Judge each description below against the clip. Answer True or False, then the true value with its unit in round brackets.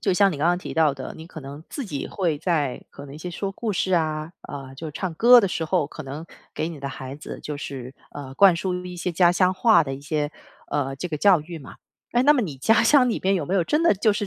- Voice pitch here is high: False (165 Hz)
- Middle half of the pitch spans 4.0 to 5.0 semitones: True (4.7 semitones)